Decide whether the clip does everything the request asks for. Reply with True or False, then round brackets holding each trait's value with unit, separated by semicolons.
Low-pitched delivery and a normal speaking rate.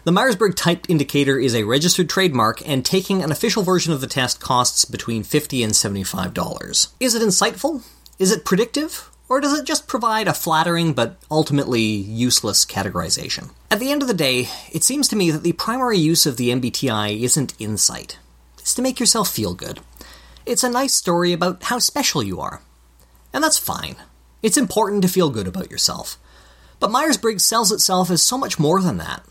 False (170 Hz; 190 wpm)